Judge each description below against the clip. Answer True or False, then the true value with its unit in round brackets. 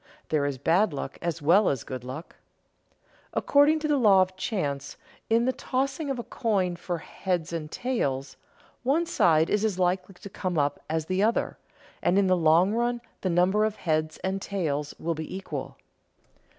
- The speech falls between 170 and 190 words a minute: True (180 wpm)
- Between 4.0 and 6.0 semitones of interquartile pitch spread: True (5.4 semitones)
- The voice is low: False (185 Hz)